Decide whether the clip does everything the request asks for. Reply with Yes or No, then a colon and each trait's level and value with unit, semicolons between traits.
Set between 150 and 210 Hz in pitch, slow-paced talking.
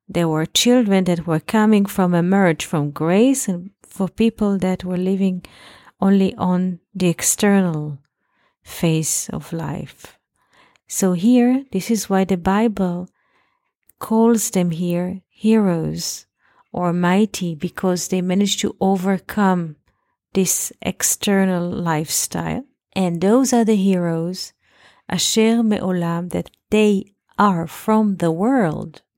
Yes: high, 190 Hz; slow, 115 wpm